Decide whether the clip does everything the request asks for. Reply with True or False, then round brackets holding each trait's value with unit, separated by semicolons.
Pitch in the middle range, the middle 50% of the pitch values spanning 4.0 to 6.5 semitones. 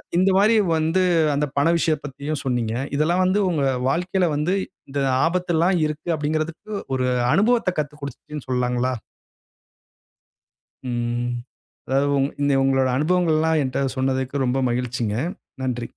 True (145 Hz; 4.4 semitones)